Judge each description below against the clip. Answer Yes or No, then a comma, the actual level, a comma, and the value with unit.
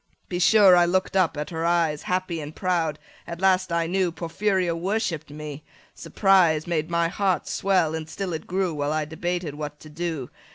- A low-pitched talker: No, medium, 170 Hz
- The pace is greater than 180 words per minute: Yes, average, 195 wpm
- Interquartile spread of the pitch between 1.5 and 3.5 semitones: Yes, average, 2.9 semitones